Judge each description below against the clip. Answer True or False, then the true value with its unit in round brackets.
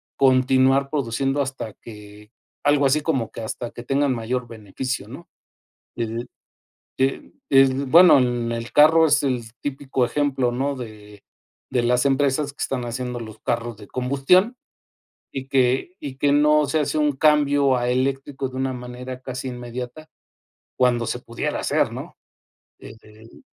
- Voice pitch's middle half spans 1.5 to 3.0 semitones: True (2.6 semitones)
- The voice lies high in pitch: False (130 Hz)